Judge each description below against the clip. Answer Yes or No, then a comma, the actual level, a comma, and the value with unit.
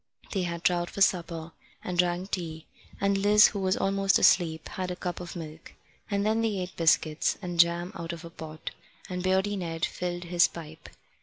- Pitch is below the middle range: No, medium, 175 Hz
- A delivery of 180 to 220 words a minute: Yes, average, 190 wpm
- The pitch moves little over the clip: Yes, narrow, 2.3 semitones